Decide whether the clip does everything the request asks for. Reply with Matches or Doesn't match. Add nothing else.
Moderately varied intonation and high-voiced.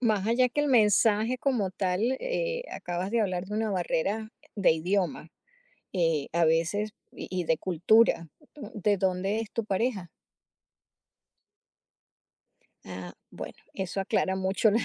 Matches